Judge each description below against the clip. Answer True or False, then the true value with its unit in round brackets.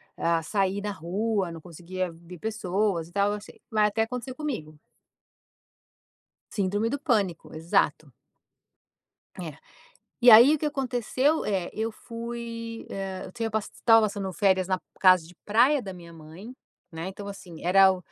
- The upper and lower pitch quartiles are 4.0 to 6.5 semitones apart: True (4.4 semitones)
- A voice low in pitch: False (200 Hz)